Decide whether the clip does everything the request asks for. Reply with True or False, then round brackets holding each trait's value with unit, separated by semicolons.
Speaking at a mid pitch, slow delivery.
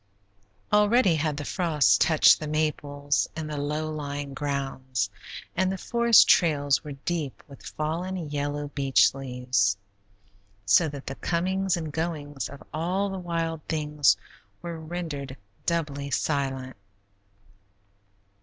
True (150 Hz; 125 wpm)